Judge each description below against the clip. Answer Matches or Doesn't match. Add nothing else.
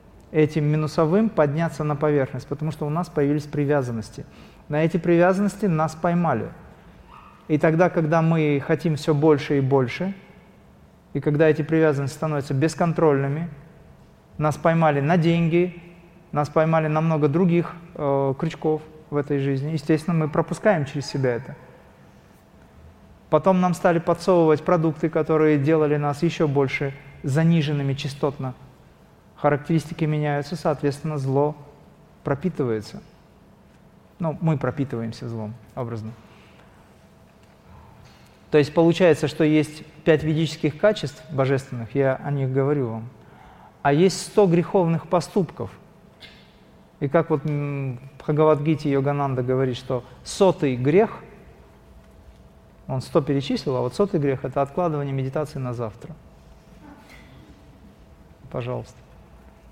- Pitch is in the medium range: Matches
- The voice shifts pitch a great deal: Doesn't match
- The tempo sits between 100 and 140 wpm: Matches